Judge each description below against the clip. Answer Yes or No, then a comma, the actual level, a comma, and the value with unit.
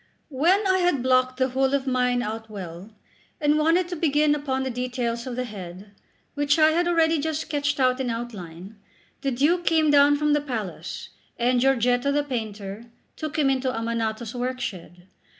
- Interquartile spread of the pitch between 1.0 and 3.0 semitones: No, average, 4.1 semitones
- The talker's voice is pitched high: Yes, very high, 260 Hz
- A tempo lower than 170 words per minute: No, average, 180 wpm